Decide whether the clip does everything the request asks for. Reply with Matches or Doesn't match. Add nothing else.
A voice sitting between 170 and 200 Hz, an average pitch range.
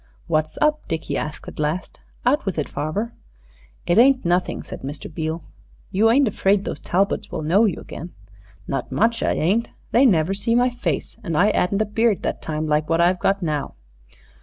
Doesn't match